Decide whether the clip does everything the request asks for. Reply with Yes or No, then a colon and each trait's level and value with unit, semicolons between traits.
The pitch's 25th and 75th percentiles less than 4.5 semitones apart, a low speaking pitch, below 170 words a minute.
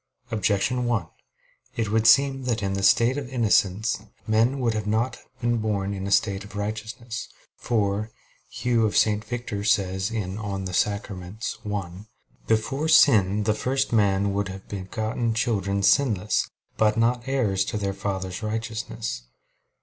Yes: average, 2.8 semitones; low, 110 Hz; average, 145 wpm